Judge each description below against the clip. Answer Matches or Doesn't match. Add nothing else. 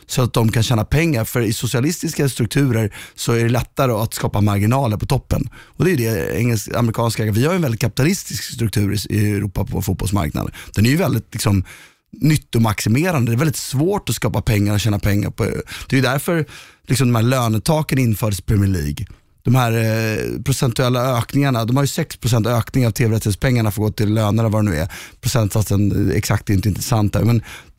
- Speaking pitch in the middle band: Doesn't match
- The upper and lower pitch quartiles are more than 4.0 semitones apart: Doesn't match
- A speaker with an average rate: Doesn't match